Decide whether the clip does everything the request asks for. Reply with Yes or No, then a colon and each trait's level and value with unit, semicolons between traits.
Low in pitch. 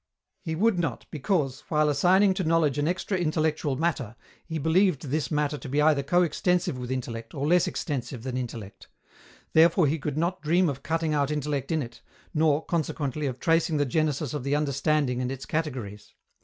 No: medium, 150 Hz